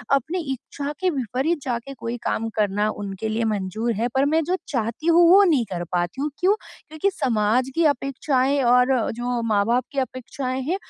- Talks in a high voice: Yes, very high, 255 Hz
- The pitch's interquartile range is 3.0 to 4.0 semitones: No, average, 4.5 semitones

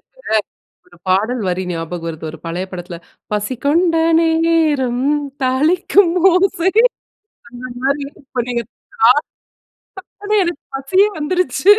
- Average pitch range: No, wide, 8.6 semitones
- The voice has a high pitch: Yes, very high, 270 Hz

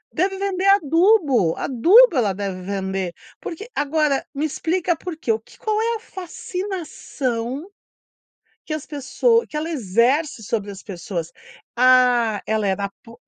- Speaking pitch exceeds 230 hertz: Yes, very high, 275 Hz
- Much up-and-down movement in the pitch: Yes, wide, 8.5 semitones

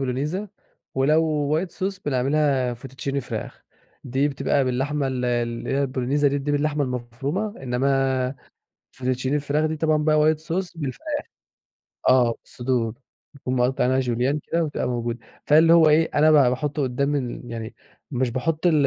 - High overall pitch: No, low, 135 Hz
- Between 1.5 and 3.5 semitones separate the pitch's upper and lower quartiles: Yes, average, 3.1 semitones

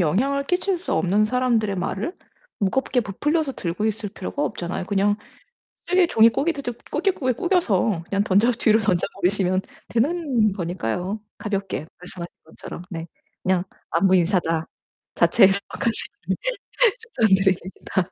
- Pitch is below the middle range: No, high, 205 Hz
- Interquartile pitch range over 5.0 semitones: Yes, wide, 5.4 semitones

